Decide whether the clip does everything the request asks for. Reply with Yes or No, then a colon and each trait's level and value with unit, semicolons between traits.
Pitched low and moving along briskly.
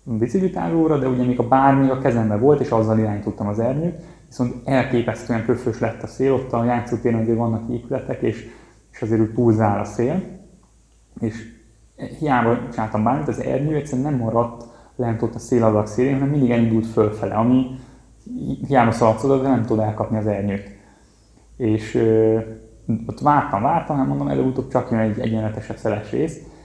Yes: low, 115 Hz; fast, 170 wpm